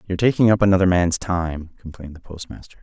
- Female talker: No, male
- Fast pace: No, average, 190 wpm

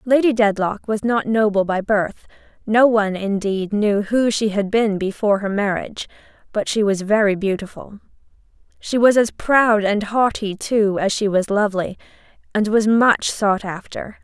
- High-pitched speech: Yes, high, 210 Hz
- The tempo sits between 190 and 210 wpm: No, average, 155 wpm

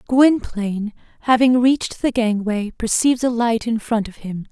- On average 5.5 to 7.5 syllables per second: No, 4.7 syllables/s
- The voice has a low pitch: No, high, 230 Hz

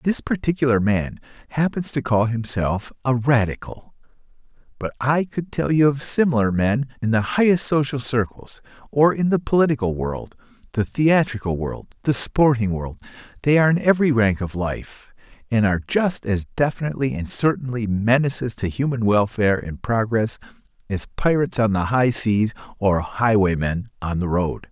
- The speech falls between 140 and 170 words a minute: Yes, average, 155 wpm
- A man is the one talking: Yes, male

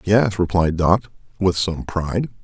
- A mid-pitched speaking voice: No, very low, 95 Hz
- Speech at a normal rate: Yes, average, 150 wpm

